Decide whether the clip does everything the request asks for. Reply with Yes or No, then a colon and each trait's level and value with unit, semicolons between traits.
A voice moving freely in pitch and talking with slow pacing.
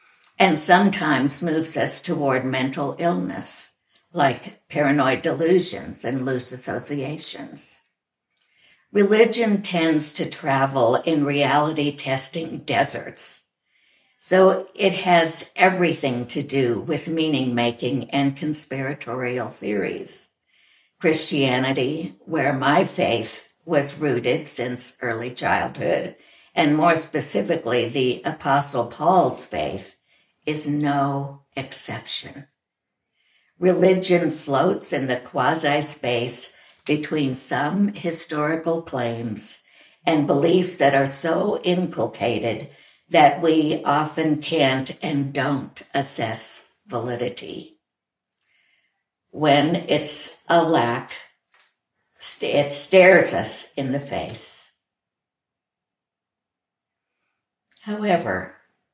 No: average, 4.0 semitones; slow, 90 wpm